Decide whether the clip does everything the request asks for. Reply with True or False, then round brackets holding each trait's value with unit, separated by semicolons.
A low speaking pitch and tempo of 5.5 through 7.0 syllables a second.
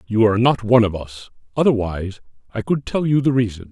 True (110 Hz; 6.3 syllables/s)